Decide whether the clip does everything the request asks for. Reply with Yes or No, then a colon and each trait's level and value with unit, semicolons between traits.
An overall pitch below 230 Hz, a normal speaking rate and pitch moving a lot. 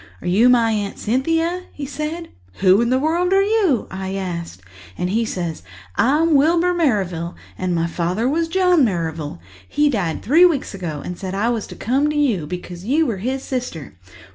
No: high, 235 Hz; average, 190 wpm; wide, 9.0 semitones